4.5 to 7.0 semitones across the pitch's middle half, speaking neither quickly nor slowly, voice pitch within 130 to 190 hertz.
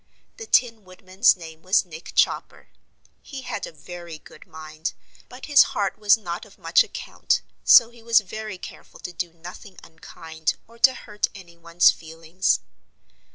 Yes: average, 5.0 semitones; average, 155 wpm; medium, 185 Hz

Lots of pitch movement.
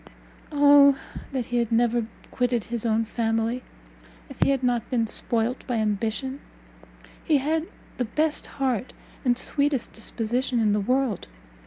No: average, 3.1 semitones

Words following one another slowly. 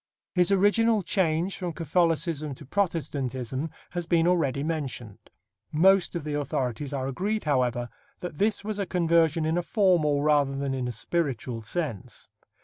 No: average, 150 wpm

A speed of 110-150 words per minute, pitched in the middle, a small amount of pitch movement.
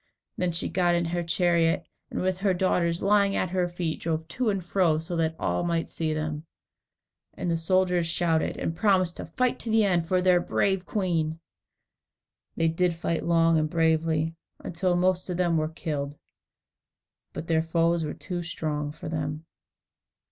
No: average, 175 wpm; medium, 170 Hz; narrow, 2.0 semitones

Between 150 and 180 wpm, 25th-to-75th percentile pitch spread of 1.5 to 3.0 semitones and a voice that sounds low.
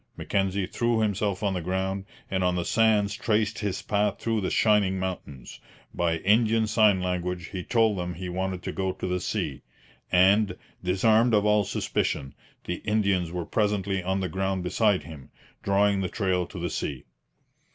Yes: average, 170 wpm; narrow, 2.6 semitones; very low, 95 Hz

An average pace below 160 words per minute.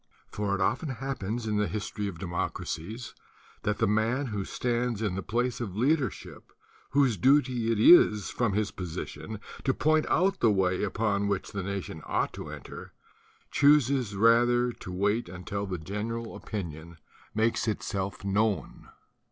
Yes: average, 150 wpm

